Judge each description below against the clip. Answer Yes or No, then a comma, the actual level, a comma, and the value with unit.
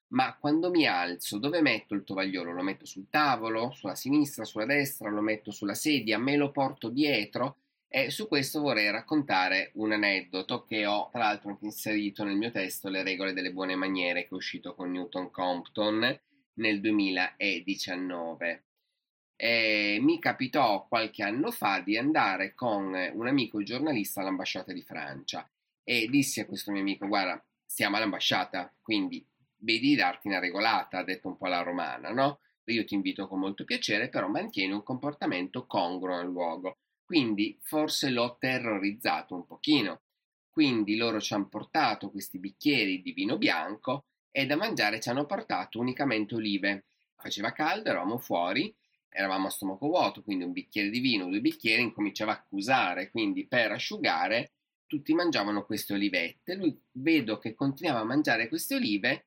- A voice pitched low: Yes, low, 110 Hz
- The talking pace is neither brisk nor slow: Yes, average, 160 wpm